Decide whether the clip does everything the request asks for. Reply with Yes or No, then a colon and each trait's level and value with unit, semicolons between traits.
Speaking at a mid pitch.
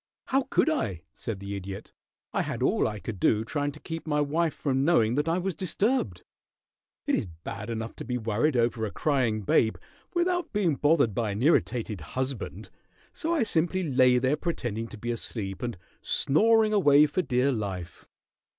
No: low, 130 Hz